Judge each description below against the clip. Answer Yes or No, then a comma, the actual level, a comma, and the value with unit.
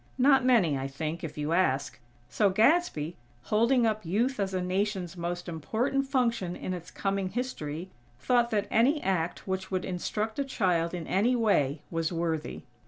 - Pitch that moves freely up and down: Yes, wide, 5.7 semitones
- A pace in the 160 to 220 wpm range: Yes, average, 170 wpm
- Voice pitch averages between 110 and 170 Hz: No, high, 190 Hz